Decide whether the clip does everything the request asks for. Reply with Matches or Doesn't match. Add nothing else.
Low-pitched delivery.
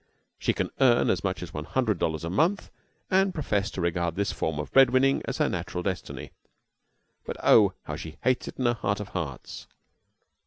Matches